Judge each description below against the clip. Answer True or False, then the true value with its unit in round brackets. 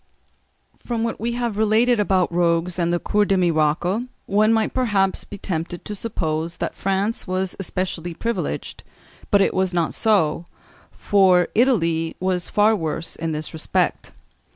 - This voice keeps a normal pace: True (155 wpm)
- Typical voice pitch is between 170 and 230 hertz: True (190 Hz)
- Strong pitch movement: False (4.1 semitones)